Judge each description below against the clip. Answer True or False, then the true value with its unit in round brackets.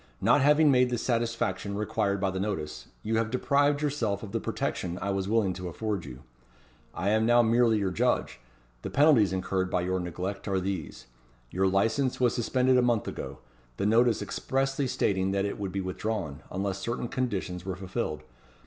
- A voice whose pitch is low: True (100 Hz)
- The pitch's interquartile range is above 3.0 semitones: True (4.2 semitones)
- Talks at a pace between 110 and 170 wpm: False (185 wpm)